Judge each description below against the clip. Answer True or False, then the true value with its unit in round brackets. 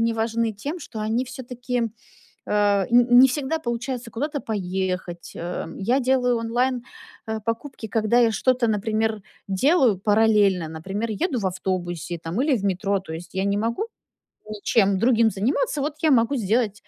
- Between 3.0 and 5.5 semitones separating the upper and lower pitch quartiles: True (4.1 semitones)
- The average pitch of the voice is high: True (225 Hz)